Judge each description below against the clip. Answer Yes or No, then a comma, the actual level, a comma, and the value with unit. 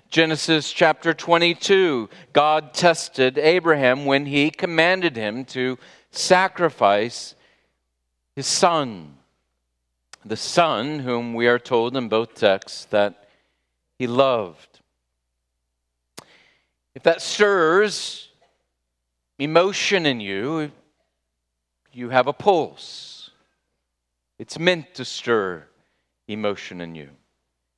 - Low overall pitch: Yes, low, 120 Hz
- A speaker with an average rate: No, slow, 95 wpm